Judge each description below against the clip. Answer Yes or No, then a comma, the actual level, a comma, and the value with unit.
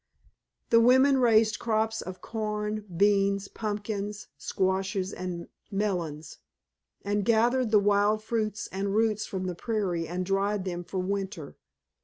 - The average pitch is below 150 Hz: No, high, 205 Hz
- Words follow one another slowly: Yes, slow, 130 wpm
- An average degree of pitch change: No, narrow, 2.3 semitones